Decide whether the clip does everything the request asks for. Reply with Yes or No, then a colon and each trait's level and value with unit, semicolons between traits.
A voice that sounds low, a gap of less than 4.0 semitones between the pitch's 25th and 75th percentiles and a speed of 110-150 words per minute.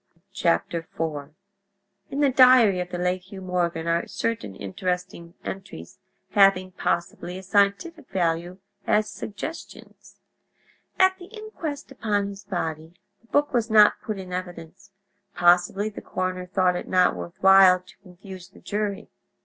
No: high, 190 Hz; average, 3.0 semitones; average, 140 wpm